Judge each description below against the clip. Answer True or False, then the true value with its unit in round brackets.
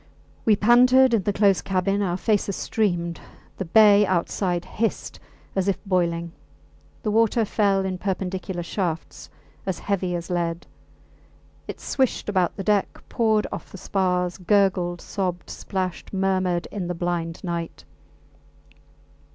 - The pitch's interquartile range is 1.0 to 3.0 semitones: True (2.7 semitones)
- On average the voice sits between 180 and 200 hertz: True (190 Hz)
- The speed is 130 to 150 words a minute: True (135 wpm)